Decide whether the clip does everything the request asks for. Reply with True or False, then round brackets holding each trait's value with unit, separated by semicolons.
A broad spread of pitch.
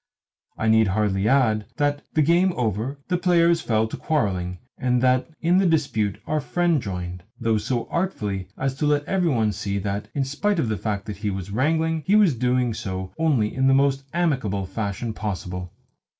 True (6.9 semitones)